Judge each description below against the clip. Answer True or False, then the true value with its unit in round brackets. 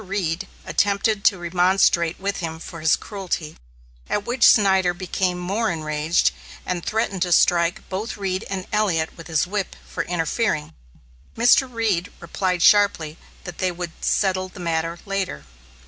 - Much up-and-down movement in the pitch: False (2.9 semitones)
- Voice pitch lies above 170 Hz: True (185 Hz)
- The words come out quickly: False (145 wpm)